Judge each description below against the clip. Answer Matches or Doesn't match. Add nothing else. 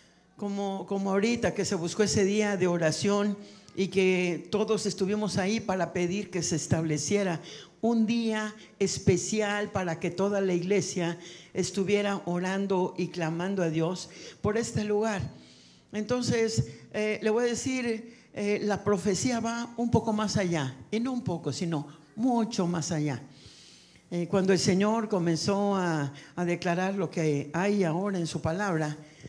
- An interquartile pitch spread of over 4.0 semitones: Doesn't match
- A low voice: Doesn't match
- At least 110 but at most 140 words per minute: Doesn't match